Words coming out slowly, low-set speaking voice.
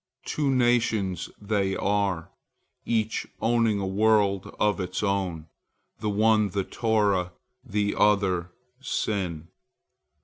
Yes: slow, 105 wpm; low, 100 Hz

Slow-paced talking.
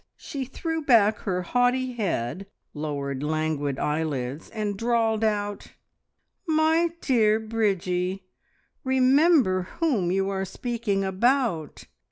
Yes: slow, 105 wpm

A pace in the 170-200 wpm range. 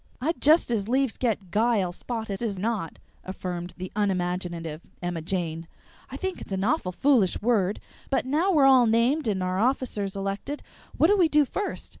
Yes: average, 175 wpm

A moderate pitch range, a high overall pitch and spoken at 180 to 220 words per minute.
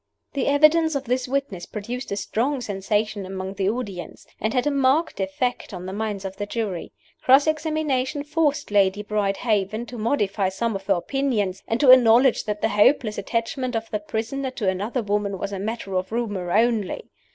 Yes: average, 4.6 semitones; high, 220 Hz; average, 185 wpm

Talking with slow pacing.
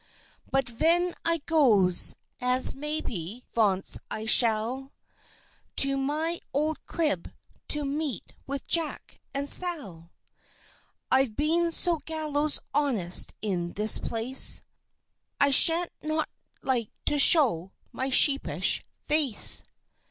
Yes: slow, 105 wpm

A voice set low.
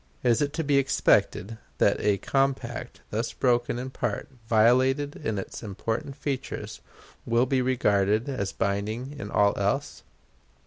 Yes: low, 120 Hz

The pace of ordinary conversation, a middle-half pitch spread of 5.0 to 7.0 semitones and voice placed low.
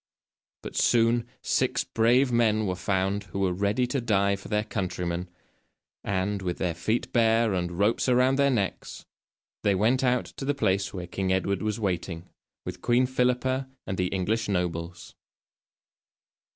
No: average, 155 wpm; average, 4.3 semitones; low, 100 Hz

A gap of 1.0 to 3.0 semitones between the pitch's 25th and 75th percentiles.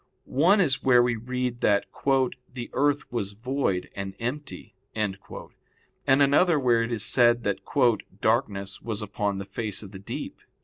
No: average, 4.3 semitones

